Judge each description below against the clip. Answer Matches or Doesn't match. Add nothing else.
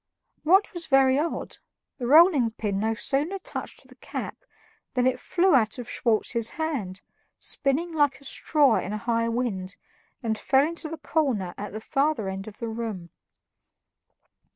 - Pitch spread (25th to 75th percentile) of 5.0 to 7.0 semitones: Matches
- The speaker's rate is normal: Matches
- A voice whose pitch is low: Doesn't match